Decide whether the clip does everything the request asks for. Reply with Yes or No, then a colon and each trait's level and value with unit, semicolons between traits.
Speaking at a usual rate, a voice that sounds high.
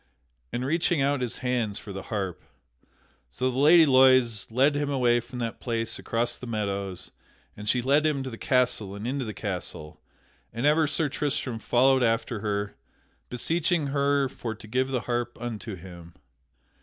No: average, 170 wpm; low, 125 Hz